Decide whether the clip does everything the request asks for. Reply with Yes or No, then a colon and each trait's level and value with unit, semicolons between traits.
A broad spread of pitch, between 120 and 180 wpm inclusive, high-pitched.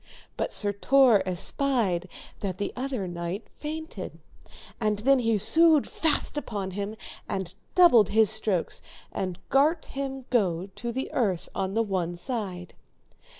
Yes: wide, 6.0 semitones; average, 140 wpm; high, 215 Hz